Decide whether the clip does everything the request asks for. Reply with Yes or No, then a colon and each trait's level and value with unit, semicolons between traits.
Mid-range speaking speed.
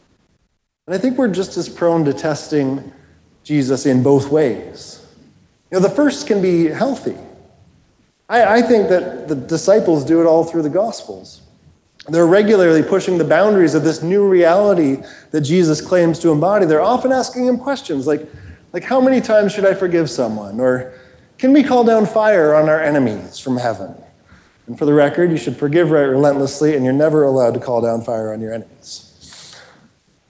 Yes: average, 180 wpm